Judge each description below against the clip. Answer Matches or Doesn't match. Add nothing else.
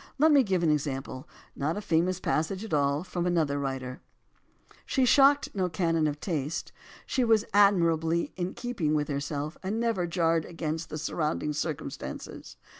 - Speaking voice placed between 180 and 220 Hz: Doesn't match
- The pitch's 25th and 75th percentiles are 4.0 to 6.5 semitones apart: Matches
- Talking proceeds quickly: Doesn't match